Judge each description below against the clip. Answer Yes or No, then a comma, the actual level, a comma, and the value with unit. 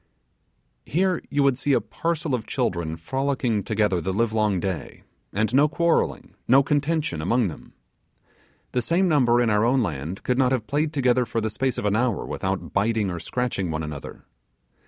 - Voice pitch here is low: Yes, low, 120 Hz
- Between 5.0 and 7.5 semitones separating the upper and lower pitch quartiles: Yes, wide, 5.6 semitones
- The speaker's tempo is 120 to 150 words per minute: No, average, 180 wpm